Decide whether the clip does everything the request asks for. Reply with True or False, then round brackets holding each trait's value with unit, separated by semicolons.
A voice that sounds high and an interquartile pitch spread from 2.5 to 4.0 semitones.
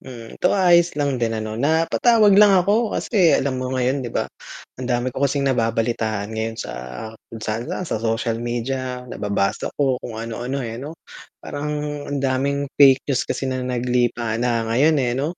False (130 Hz; 3.7 semitones)